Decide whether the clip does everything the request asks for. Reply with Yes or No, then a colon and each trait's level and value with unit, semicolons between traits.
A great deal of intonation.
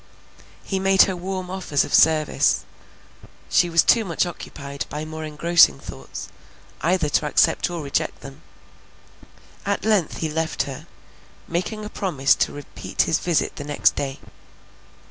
No: average, 3.9 semitones